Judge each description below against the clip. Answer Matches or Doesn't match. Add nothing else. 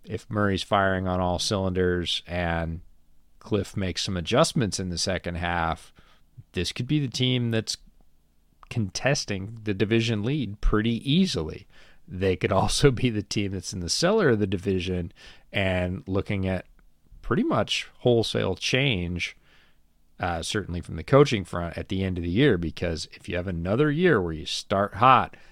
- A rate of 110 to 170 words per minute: Matches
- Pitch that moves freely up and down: Doesn't match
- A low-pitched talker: Matches